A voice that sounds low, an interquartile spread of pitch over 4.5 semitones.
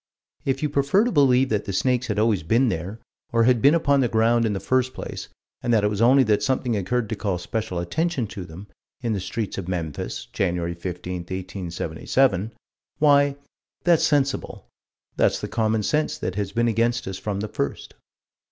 Yes: low, 110 Hz; average, 5.2 semitones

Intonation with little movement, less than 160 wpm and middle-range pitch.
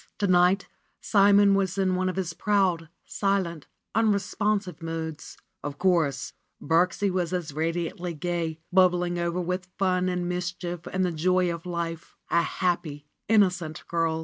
Yes: narrow, 2.0 semitones; average, 150 wpm; medium, 180 Hz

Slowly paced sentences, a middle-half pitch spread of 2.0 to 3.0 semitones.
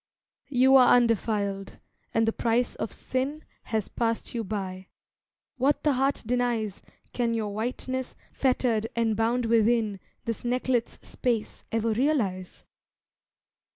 Yes: slow, 120 wpm; narrow, 2.4 semitones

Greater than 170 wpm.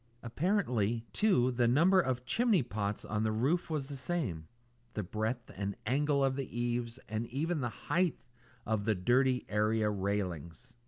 No: average, 160 wpm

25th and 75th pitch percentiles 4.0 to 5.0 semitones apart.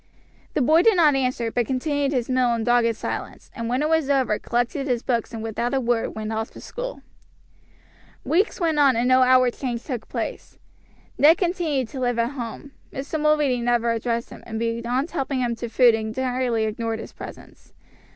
No: average, 3.2 semitones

